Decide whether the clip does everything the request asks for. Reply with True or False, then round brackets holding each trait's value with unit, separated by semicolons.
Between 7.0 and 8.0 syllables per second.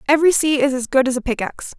True (7.5 syllables/s)